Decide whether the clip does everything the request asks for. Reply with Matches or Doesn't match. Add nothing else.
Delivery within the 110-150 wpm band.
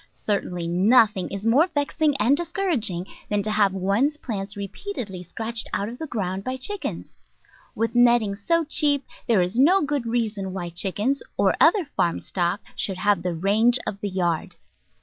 Doesn't match